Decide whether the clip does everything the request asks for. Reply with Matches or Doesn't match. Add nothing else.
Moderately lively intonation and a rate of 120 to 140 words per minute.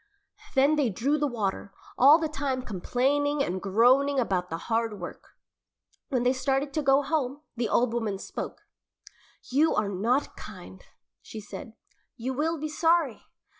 Doesn't match